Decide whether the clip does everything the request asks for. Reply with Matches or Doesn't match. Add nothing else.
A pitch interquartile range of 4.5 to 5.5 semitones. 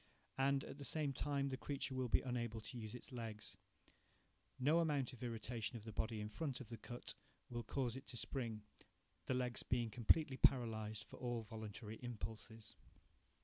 Doesn't match